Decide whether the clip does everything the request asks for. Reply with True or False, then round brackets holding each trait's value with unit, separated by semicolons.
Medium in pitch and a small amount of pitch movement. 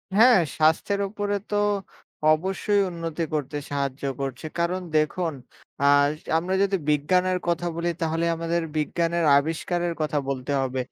False (165 Hz; 3.3 semitones)